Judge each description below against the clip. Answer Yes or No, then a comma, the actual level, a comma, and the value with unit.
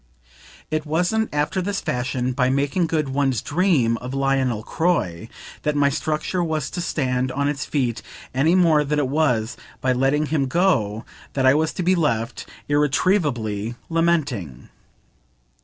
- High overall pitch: No, medium, 145 Hz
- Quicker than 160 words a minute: No, average, 150 wpm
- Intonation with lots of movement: No, average, 3.9 semitones